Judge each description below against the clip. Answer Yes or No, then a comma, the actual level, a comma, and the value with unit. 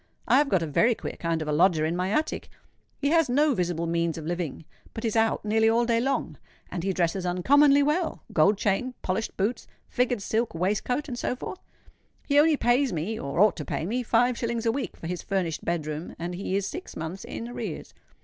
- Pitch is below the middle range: No, high, 210 Hz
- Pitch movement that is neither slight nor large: No, wide, 6.3 semitones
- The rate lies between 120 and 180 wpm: No, average, 200 wpm